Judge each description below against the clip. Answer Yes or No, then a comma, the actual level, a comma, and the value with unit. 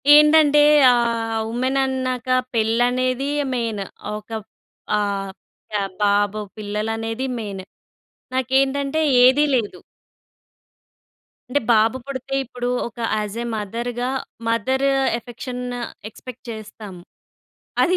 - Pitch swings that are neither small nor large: Yes, average, 3.2 semitones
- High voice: Yes, high, 240 Hz